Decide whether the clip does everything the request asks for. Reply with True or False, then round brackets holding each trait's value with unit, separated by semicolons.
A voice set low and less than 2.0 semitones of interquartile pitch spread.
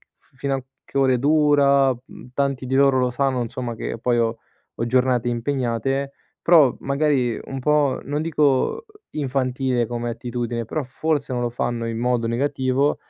False (130 Hz; 2.5 semitones)